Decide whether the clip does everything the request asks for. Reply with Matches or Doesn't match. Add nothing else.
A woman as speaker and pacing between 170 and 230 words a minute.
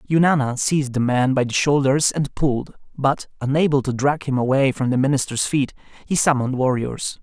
Doesn't match